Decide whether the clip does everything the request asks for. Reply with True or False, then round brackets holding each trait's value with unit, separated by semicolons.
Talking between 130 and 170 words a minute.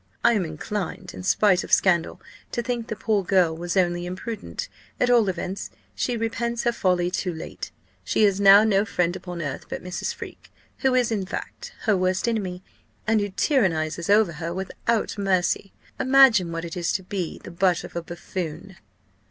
False (185 wpm)